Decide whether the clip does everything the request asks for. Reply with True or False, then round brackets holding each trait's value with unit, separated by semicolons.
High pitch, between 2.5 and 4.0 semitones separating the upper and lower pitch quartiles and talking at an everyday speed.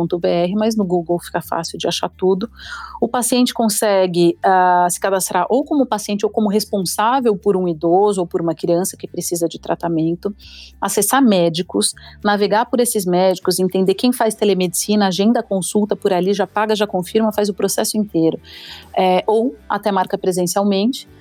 True (195 Hz; 3.2 semitones; 165 wpm)